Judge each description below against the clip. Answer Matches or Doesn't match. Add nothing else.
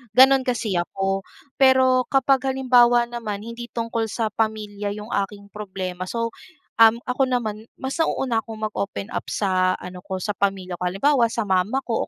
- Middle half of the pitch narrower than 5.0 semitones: Matches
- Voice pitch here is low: Doesn't match